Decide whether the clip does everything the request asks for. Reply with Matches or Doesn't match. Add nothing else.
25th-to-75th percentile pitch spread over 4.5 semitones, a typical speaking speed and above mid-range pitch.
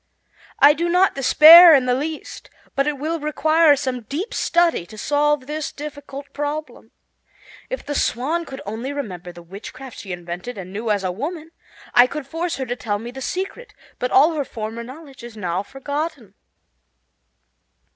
Matches